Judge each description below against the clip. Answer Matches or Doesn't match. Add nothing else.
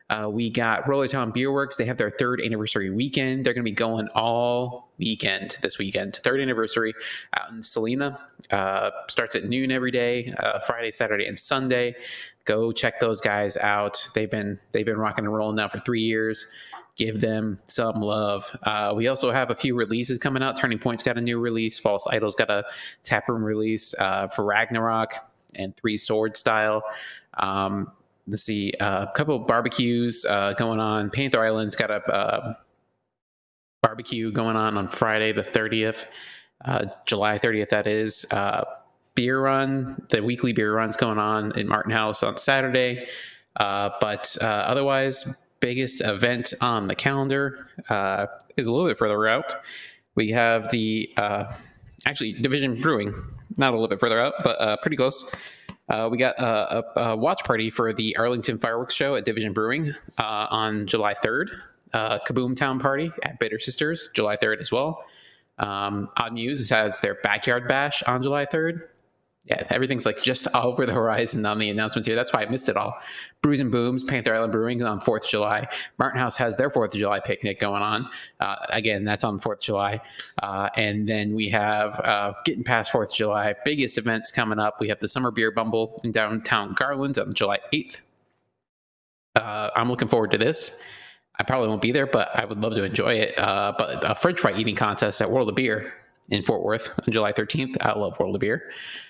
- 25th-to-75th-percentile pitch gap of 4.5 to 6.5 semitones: Doesn't match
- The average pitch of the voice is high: Doesn't match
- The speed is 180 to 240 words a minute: Matches